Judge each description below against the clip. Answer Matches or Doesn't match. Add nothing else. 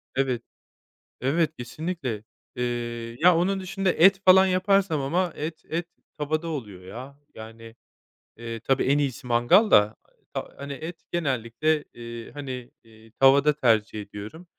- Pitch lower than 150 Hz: Matches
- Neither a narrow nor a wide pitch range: Doesn't match